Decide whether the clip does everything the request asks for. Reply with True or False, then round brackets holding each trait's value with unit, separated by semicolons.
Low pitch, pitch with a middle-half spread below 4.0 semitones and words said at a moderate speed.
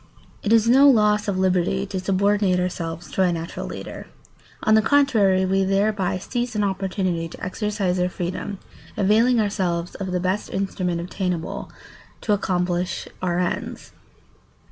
False (190 Hz; 2.6 semitones; 150 wpm)